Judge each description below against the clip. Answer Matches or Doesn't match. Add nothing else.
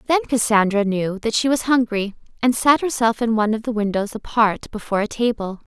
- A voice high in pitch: Matches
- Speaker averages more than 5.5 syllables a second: Matches